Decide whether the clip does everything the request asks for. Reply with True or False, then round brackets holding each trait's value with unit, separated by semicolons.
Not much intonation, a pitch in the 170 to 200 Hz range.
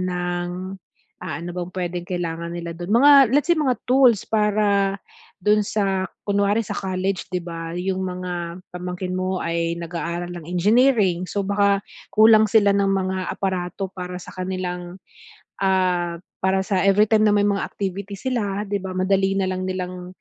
True (2.3 semitones; 190 Hz)